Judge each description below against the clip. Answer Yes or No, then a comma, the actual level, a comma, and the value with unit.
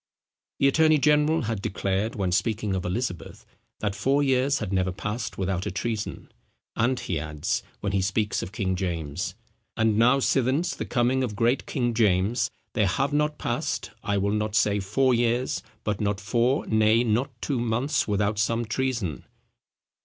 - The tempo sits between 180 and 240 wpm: No, average, 170 wpm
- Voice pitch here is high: No, low, 110 Hz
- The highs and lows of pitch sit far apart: No, average, 4.4 semitones